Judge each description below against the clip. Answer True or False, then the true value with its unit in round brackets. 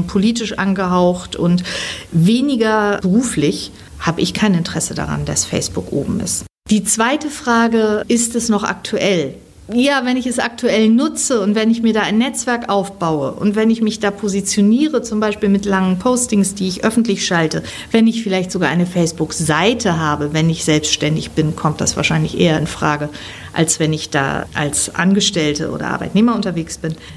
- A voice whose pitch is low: False (200 Hz)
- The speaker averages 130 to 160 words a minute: False (170 wpm)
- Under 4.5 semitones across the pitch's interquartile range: False (5.2 semitones)